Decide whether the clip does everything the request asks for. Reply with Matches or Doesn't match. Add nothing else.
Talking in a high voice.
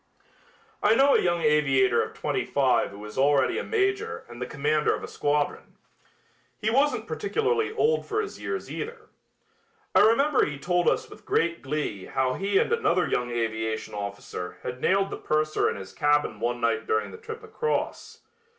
Doesn't match